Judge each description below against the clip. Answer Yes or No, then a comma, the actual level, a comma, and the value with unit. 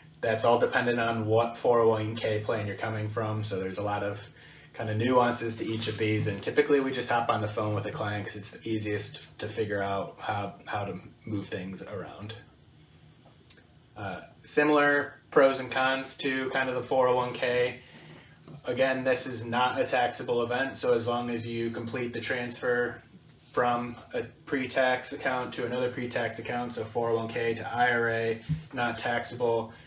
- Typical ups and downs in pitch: No, narrow, 2.1 semitones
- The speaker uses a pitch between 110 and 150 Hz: Yes, low, 120 Hz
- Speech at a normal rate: Yes, average, 175 wpm